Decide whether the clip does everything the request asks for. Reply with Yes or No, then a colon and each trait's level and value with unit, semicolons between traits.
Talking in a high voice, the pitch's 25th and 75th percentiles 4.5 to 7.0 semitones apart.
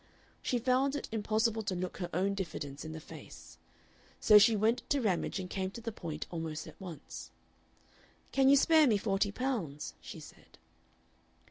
Yes: high, 200 Hz; average, 5.1 semitones